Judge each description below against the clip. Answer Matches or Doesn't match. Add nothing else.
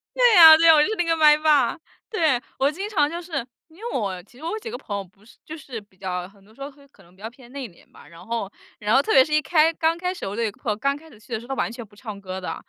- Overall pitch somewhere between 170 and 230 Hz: Doesn't match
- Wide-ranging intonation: Matches